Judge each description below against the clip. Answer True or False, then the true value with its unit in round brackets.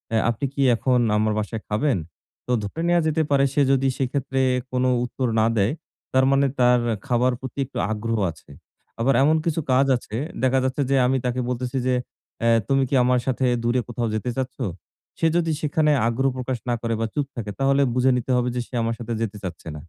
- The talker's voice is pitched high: False (125 Hz)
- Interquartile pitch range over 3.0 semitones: False (2.7 semitones)